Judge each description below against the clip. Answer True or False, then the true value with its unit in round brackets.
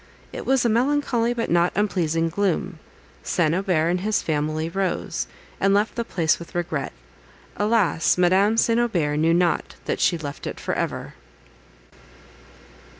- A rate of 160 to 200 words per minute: False (150 wpm)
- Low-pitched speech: False (180 Hz)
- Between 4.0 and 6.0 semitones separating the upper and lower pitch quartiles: True (4.7 semitones)